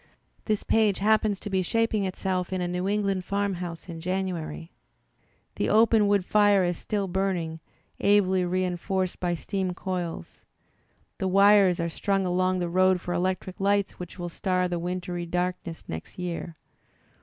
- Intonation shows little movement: Yes, narrow, 2.0 semitones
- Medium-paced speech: Yes, average, 155 wpm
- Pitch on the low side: No, medium, 185 Hz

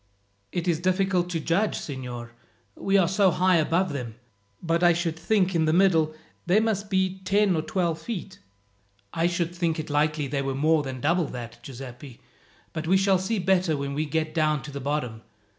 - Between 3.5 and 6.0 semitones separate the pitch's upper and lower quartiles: Yes, average, 4.1 semitones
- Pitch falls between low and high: Yes, medium, 165 Hz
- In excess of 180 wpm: Yes, average, 190 wpm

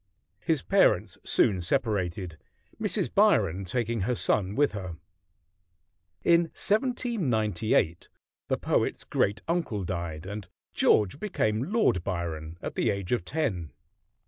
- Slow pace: Yes, slow, 120 wpm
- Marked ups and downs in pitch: Yes, wide, 6.3 semitones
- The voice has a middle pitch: No, low, 105 Hz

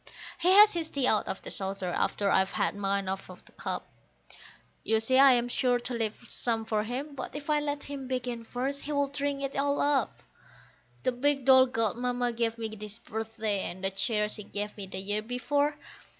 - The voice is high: Yes, high, 245 Hz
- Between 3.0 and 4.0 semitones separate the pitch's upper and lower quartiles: No, average, 4.7 semitones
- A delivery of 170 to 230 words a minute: Yes, fast, 205 wpm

